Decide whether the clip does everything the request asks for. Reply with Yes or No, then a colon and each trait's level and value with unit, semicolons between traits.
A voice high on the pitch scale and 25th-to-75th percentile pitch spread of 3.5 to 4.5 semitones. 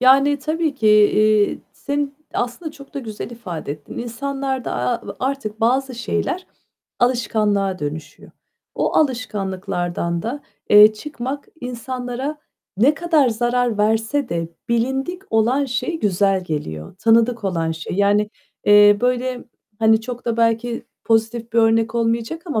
Yes: high, 230 Hz; average, 4.0 semitones